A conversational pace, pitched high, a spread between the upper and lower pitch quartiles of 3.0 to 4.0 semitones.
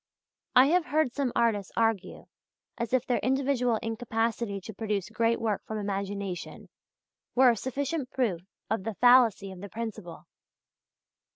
Yes: average, 145 wpm; high, 225 Hz; average, 3.7 semitones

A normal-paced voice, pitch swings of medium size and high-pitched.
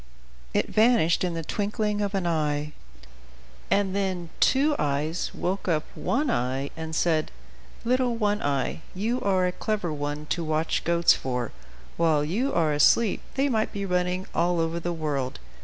No: average, 160 wpm; average, 5.0 semitones; medium, 175 Hz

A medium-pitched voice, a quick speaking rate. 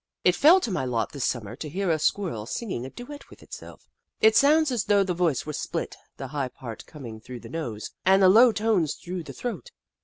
Yes: medium, 175 Hz; fast, 225 wpm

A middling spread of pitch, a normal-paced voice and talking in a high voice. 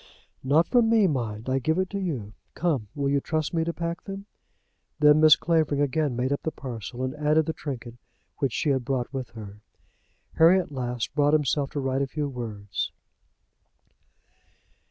No: average, 4.0 semitones; average, 180 wpm; medium, 145 Hz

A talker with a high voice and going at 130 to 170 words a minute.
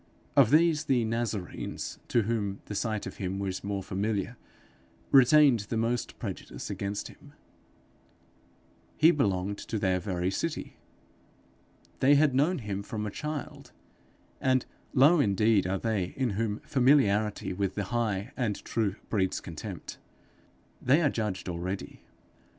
No: low, 110 Hz; slow, 135 wpm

